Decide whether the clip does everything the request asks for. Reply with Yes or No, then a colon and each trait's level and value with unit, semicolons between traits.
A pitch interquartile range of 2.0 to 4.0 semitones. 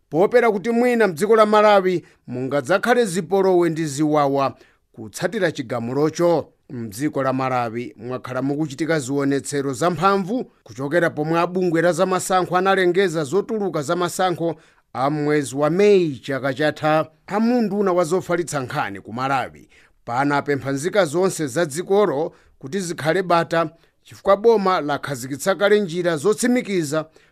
No: average, 5.2 semitones